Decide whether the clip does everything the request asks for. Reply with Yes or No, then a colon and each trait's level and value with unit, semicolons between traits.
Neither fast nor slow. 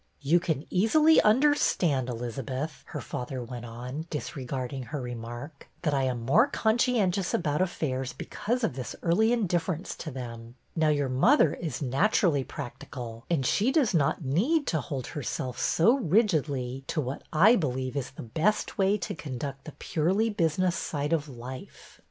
Yes: average, 155 wpm